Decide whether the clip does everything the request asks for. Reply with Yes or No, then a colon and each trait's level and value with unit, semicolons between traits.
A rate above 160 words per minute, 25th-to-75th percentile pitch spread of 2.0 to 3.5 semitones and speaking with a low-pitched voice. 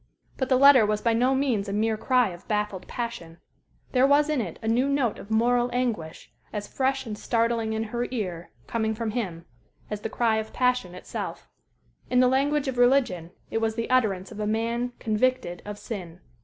No: average, 195 wpm; average, 3.2 semitones; high, 225 Hz